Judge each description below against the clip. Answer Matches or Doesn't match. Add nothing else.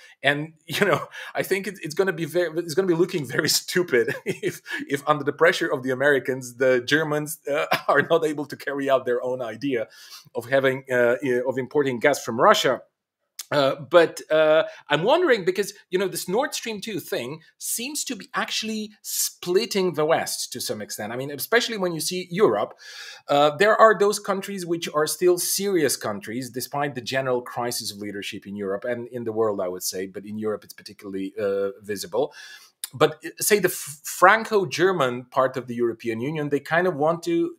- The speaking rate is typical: Matches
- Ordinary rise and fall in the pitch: Doesn't match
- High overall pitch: Doesn't match